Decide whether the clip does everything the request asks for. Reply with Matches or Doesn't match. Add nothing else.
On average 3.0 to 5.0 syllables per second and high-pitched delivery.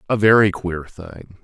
Doesn't match